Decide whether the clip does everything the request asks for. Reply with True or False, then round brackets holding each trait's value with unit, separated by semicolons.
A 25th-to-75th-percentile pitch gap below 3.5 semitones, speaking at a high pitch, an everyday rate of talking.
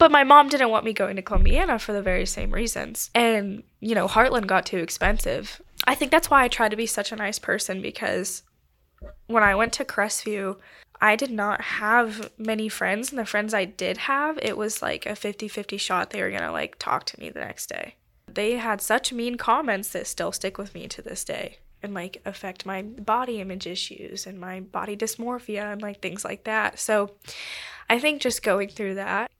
False (2.7 semitones; 215 Hz; 215 wpm)